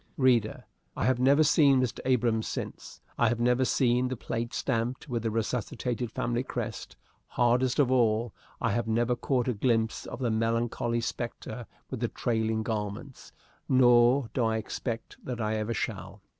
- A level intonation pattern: Yes, narrow, 2.0 semitones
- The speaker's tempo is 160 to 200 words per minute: Yes, average, 165 wpm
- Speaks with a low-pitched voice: Yes, low, 120 Hz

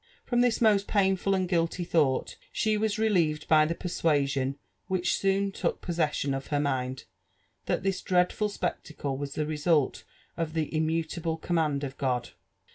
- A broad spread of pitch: No, average, 4.8 semitones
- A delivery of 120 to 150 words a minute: No, average, 160 wpm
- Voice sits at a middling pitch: Yes, medium, 165 Hz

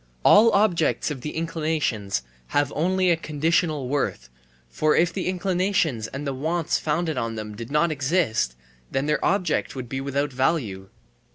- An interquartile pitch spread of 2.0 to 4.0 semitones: No, average, 4.7 semitones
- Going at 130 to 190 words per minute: Yes, average, 160 wpm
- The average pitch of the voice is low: No, medium, 150 Hz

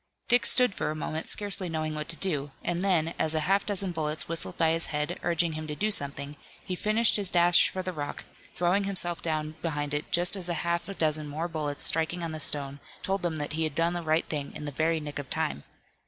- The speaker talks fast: Yes, fast, 245 wpm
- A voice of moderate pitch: Yes, medium, 165 Hz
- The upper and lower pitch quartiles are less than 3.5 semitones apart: Yes, narrow, 2.6 semitones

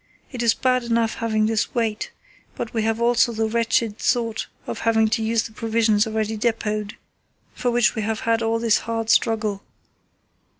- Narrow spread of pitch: Yes, narrow, 1.0 semitones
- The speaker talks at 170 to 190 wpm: Yes, average, 180 wpm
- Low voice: No, high, 225 Hz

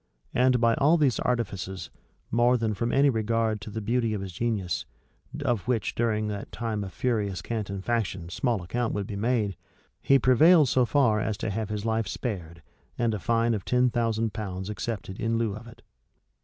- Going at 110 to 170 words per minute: No, average, 195 wpm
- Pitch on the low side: Yes, low, 115 Hz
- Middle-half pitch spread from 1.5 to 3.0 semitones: Yes, average, 2.7 semitones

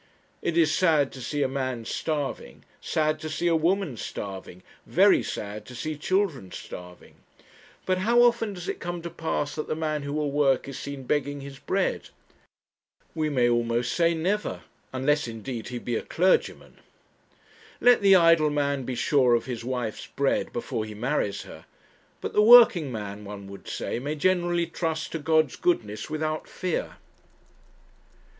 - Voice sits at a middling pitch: Yes, medium, 145 Hz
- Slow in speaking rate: No, average, 165 wpm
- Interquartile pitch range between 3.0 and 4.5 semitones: No, average, 5.3 semitones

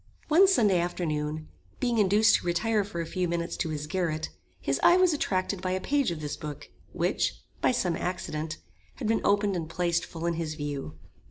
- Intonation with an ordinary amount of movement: Yes, average, 4.6 semitones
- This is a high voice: No, medium, 175 Hz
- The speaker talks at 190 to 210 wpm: Yes, average, 195 wpm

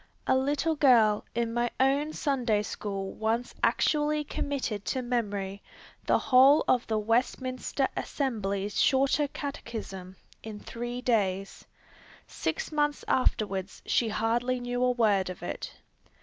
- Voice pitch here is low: No, high, 240 Hz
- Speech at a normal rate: No, slow, 125 wpm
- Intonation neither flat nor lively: Yes, average, 4.2 semitones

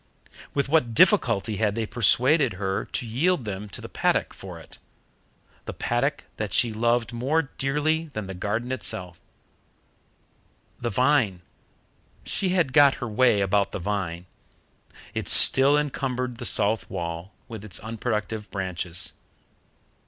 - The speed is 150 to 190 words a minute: No, slow, 135 wpm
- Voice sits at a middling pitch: No, low, 115 Hz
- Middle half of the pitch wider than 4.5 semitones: Yes, average, 5.0 semitones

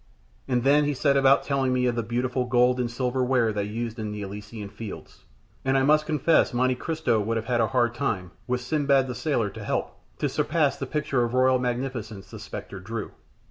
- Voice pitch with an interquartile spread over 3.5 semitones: No, average, 2.9 semitones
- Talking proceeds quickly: Yes, fast, 215 wpm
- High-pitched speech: No, low, 125 Hz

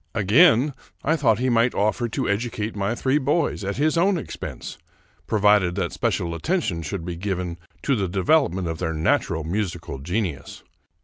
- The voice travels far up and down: Yes, wide, 6.5 semitones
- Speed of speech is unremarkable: Yes, average, 165 wpm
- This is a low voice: Yes, low, 105 Hz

